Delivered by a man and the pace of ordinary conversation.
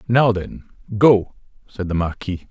Yes: male; average, 145 wpm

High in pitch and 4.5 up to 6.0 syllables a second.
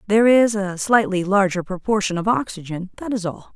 Yes: high, 195 Hz; 5.5 syllables/s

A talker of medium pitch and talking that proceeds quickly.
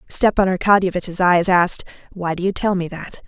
No: medium, 180 Hz; average, 185 wpm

